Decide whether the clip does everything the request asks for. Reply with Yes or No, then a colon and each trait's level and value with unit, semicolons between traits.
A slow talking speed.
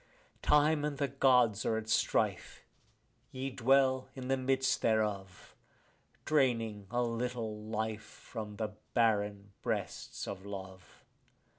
Yes: slow, 120 wpm